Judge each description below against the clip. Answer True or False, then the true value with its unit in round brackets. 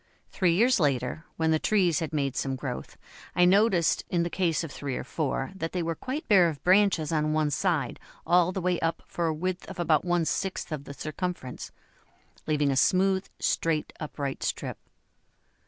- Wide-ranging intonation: False (3.3 semitones)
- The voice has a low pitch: False (165 Hz)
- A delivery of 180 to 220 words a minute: True (190 wpm)